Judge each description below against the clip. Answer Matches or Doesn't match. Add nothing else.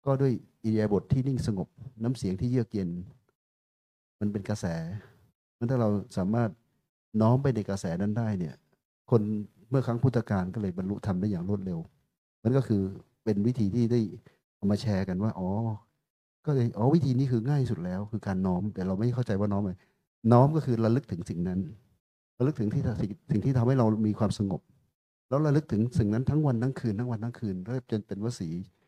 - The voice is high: Doesn't match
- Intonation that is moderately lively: Matches